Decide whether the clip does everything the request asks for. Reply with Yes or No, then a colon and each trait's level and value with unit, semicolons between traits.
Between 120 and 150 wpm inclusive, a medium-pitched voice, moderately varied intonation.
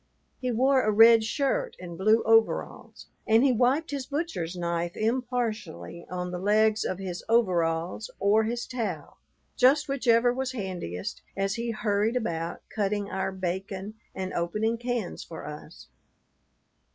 No: average, 140 wpm; high, 215 Hz; average, 4.9 semitones